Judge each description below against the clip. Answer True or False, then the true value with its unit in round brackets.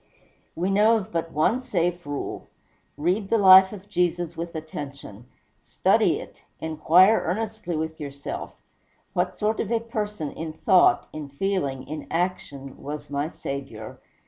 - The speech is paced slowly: False (145 wpm)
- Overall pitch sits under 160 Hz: False (170 Hz)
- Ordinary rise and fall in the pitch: True (5.0 semitones)